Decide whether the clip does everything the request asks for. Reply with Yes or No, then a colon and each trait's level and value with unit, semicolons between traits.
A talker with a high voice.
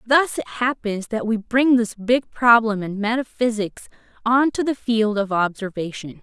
Yes: high, 225 Hz